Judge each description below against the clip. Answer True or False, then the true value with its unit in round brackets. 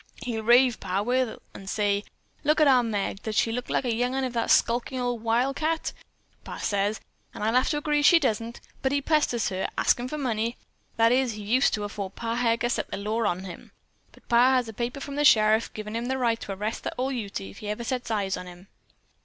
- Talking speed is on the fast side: True (230 wpm)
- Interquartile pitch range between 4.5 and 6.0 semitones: False (3.3 semitones)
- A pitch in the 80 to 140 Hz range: False (230 Hz)